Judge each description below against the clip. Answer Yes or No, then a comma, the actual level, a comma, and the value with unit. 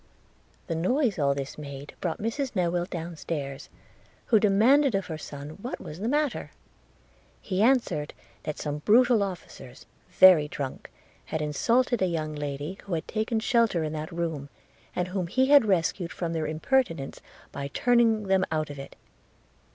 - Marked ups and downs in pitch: Yes, wide, 6.5 semitones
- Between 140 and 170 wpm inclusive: Yes, average, 160 wpm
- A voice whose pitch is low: No, medium, 175 Hz